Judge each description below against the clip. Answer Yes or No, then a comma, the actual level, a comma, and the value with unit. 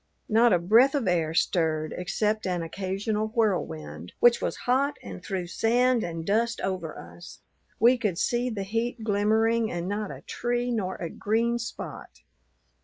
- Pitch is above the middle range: Yes, high, 210 Hz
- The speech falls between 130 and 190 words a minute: Yes, average, 160 wpm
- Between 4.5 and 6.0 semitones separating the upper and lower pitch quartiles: Yes, average, 4.9 semitones